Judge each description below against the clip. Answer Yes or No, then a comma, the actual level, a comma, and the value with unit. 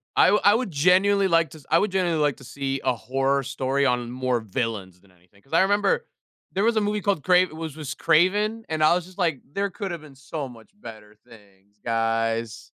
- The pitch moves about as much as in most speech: No, wide, 7.9 semitones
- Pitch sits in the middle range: Yes, medium, 145 Hz